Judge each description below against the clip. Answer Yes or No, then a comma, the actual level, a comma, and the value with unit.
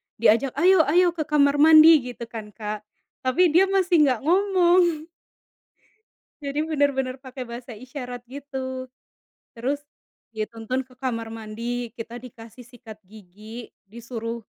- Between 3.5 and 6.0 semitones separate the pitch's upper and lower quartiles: Yes, average, 4.7 semitones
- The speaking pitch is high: Yes, very high, 255 Hz